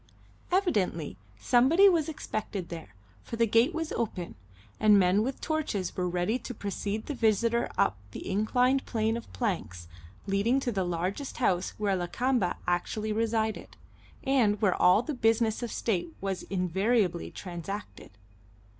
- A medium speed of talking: Yes, average, 145 wpm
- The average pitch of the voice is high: Yes, high, 215 Hz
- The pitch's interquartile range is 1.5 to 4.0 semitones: No, average, 4.8 semitones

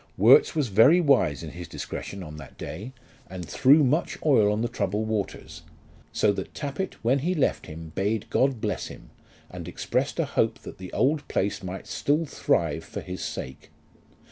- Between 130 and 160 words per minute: No, average, 180 wpm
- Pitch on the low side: Yes, low, 110 Hz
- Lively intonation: Yes, wide, 7.2 semitones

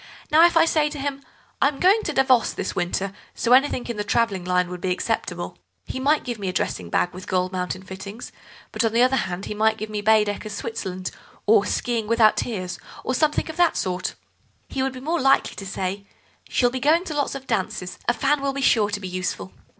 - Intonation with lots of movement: Yes, wide, 6.3 semitones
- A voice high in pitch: Yes, high, 220 Hz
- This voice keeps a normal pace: No, fast, 230 wpm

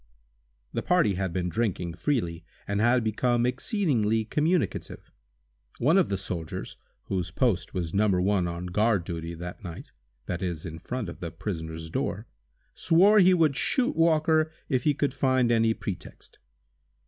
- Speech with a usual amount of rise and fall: No, wide, 7.0 semitones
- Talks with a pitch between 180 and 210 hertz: No, low, 105 Hz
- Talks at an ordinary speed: Yes, average, 150 wpm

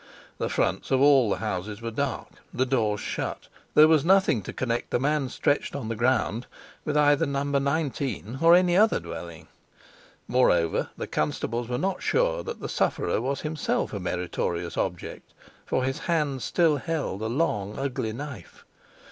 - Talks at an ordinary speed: Yes, average, 165 wpm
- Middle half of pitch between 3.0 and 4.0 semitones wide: No, wide, 5.4 semitones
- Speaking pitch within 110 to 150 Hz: Yes, low, 135 Hz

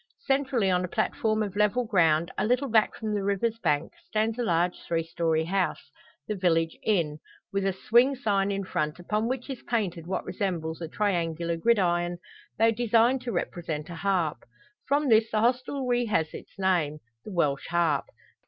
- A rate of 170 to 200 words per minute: Yes, average, 175 wpm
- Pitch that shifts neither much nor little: Yes, average, 5.0 semitones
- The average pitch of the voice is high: Yes, high, 195 Hz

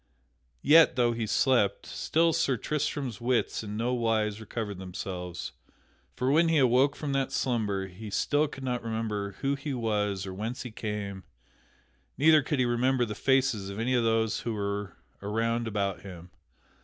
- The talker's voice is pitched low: Yes, low, 115 Hz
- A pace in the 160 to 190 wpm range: Yes, average, 170 wpm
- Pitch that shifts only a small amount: No, average, 4.3 semitones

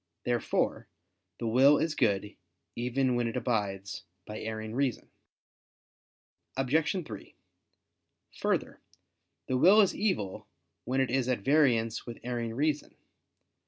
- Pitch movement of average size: Yes, average, 3.6 semitones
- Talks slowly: Yes, slow, 120 wpm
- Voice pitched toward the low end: Yes, low, 125 Hz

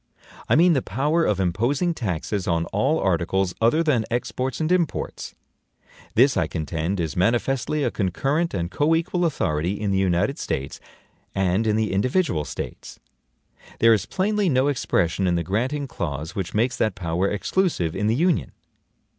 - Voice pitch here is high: No, low, 110 Hz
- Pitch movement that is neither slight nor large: No, wide, 8.2 semitones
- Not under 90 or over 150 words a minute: No, average, 160 wpm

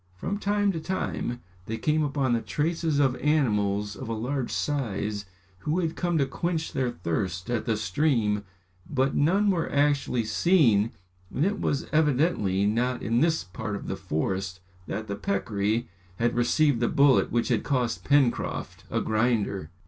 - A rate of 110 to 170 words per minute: Yes, average, 165 wpm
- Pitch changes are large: Yes, wide, 6.2 semitones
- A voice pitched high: No, low, 125 Hz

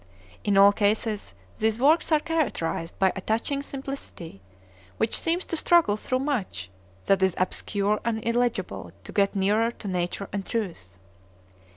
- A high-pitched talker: Yes, high, 210 Hz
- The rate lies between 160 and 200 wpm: No, average, 150 wpm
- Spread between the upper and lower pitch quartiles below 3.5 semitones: No, average, 4.8 semitones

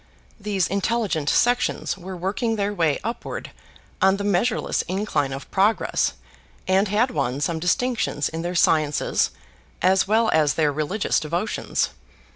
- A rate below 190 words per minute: Yes, slow, 135 wpm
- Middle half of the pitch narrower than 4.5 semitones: No, average, 5.0 semitones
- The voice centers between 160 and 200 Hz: Yes, high, 190 Hz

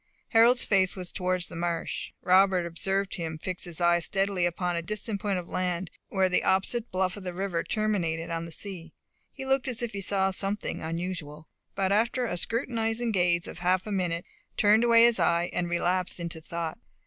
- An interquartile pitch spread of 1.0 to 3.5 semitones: Yes, average, 3.1 semitones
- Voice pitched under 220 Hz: Yes, medium, 185 Hz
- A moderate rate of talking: Yes, average, 195 wpm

